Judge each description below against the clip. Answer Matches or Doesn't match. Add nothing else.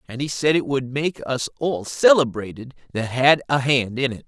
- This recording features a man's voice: Matches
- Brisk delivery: Matches